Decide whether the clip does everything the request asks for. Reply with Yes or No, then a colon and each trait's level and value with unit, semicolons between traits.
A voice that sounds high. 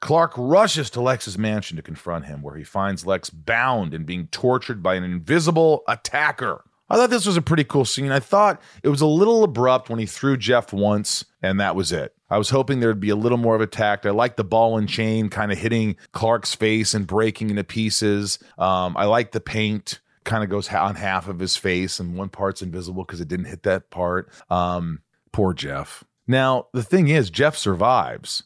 No: low, 110 Hz